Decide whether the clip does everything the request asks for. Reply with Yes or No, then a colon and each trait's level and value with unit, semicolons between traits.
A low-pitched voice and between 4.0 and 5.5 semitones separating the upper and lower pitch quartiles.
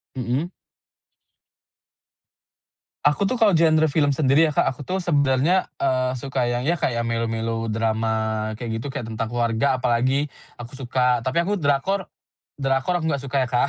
Yes: low, 130 Hz; average, 4.6 semitones